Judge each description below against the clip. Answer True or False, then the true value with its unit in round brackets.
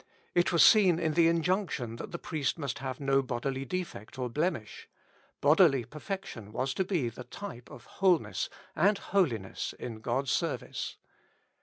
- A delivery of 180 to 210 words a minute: False (160 wpm)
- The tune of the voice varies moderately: False (6.2 semitones)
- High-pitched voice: False (140 Hz)